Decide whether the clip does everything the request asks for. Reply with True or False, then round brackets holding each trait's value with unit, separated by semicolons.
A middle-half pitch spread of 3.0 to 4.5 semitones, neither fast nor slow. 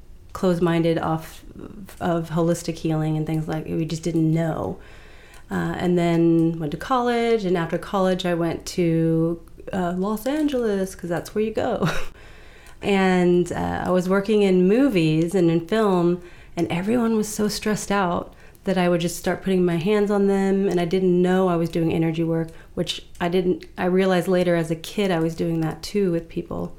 False (2.5 semitones; 190 wpm)